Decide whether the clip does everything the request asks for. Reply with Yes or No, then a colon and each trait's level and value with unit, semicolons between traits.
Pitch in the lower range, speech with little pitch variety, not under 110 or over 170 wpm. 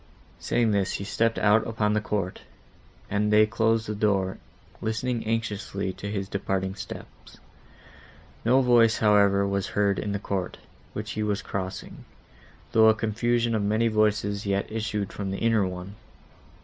Yes: low, 105 Hz; narrow, 2.0 semitones; average, 155 wpm